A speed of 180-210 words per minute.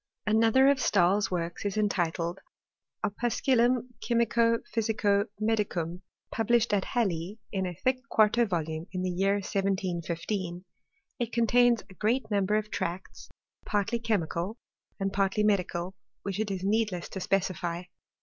No: average, 140 wpm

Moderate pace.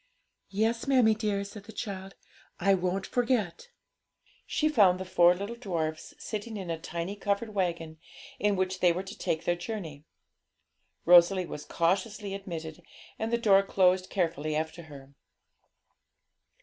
Yes: average, 145 wpm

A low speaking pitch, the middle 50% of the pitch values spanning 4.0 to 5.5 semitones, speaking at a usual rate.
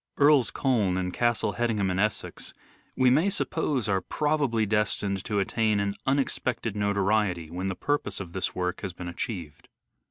Yes: low, 105 Hz; average, 4.5 semitones; average, 160 wpm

